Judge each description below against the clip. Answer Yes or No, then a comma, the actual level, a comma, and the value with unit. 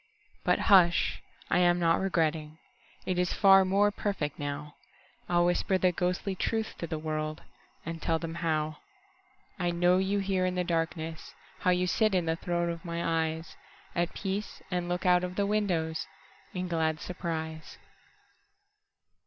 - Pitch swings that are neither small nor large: No, narrow, 2.2 semitones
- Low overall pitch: No, medium, 175 Hz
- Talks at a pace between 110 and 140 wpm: Yes, slow, 135 wpm